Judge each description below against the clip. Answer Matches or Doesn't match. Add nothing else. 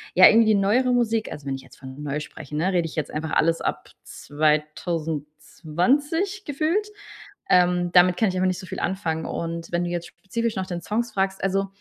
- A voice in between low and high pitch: Matches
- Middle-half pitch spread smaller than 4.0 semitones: Doesn't match